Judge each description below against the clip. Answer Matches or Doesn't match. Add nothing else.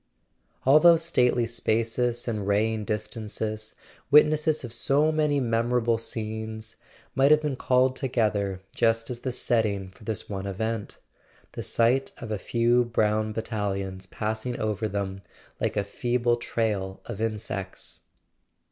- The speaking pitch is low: Matches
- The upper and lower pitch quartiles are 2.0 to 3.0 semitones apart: Matches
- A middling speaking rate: Doesn't match